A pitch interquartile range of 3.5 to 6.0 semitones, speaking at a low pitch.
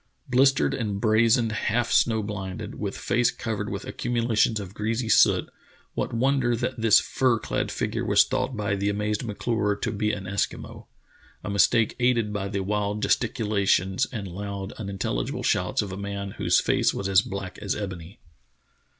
No: narrow, 2.6 semitones; low, 105 Hz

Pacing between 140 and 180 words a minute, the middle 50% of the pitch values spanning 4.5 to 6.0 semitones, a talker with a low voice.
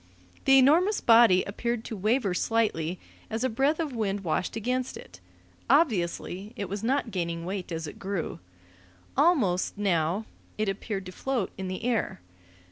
No: average, 155 wpm; average, 5.2 semitones; high, 210 Hz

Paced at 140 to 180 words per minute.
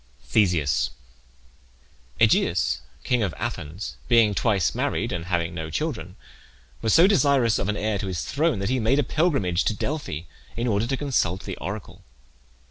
Yes: average, 160 wpm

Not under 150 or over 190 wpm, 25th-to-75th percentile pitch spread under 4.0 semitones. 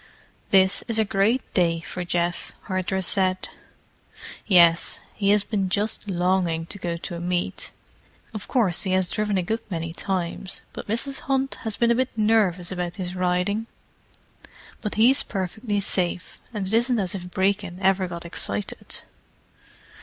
Yes: average, 155 wpm; average, 3.0 semitones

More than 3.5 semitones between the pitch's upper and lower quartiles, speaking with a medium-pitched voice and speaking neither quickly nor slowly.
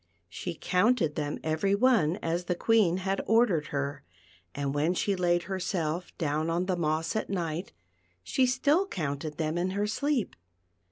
Yes: average, 4.3 semitones; medium, 175 Hz; average, 160 wpm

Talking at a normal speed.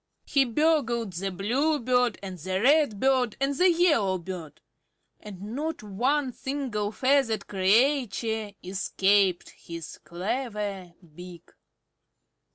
No: slow, 95 wpm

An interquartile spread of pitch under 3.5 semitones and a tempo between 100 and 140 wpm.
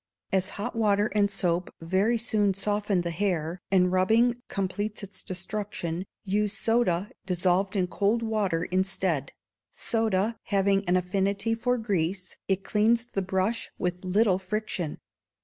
Yes: narrow, 2.6 semitones; slow, 135 wpm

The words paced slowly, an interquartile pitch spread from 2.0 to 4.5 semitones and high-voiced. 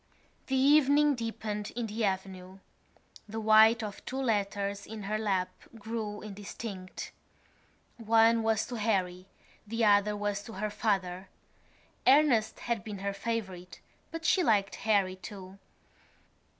Yes: slow, 130 wpm; narrow, 2.5 semitones; high, 210 Hz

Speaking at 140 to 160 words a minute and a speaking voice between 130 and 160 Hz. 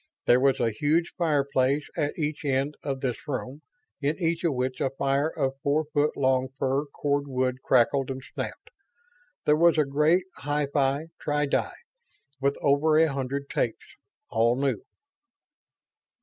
Yes: average, 150 wpm; medium, 140 Hz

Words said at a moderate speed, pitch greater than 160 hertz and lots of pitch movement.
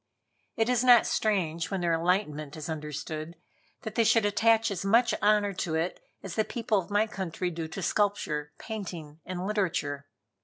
No: average, 170 wpm; high, 190 Hz; average, 4.8 semitones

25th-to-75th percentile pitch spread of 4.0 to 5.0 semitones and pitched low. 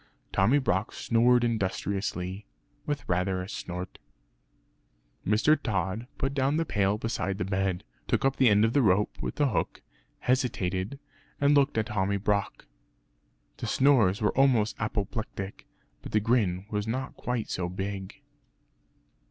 Yes: average, 4.4 semitones; low, 105 Hz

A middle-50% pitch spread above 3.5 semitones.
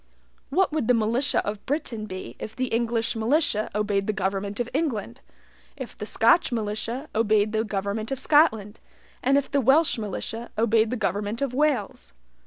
Yes: average, 3.9 semitones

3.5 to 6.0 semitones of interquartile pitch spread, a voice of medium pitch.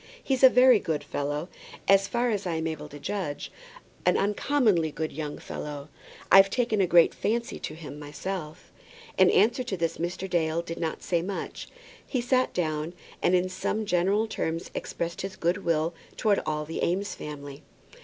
Yes: average, 4.4 semitones; medium, 175 Hz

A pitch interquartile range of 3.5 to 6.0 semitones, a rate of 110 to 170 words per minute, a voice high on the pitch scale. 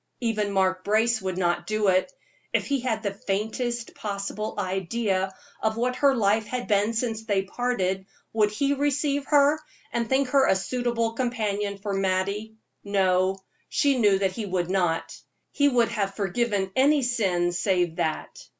Yes: average, 3.9 semitones; average, 160 wpm; high, 210 Hz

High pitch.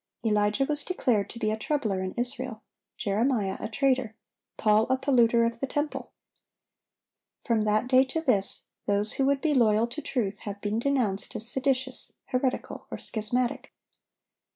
Yes: high, 235 Hz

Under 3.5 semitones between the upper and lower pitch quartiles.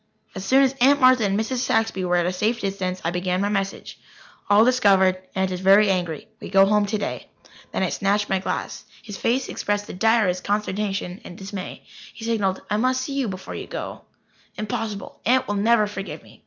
Yes: average, 2.8 semitones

